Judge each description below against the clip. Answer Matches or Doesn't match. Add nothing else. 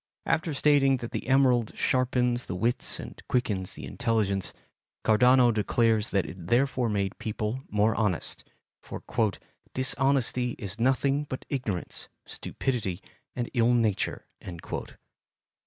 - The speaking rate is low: Matches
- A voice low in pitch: Matches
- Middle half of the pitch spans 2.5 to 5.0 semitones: Matches